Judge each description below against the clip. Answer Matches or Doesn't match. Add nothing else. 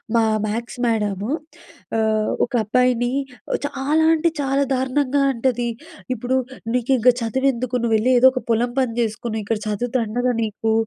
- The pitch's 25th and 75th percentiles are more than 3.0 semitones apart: Doesn't match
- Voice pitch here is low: Doesn't match